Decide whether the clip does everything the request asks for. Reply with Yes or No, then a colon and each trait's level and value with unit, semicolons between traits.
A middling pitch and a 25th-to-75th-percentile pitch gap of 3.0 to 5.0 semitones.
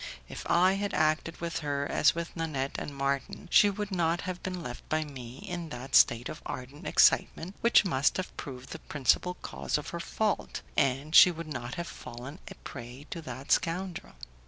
Yes: medium, 155 Hz; average, 4.6 semitones